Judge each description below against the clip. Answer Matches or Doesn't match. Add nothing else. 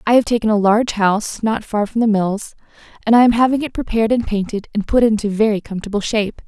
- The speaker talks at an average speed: Doesn't match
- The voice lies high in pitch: Matches